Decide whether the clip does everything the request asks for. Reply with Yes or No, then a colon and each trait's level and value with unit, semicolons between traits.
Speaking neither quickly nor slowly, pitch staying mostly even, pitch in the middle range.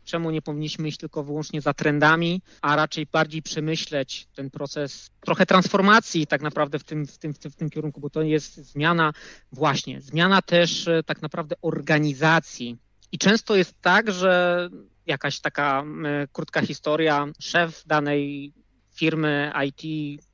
Yes: average, 150 wpm; narrow, 2.3 semitones; medium, 155 Hz